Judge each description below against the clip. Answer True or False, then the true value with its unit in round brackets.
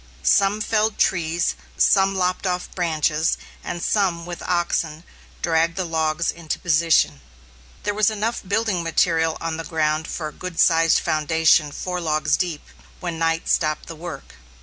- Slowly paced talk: False (155 wpm)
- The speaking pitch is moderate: True (165 Hz)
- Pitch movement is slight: True (2.3 semitones)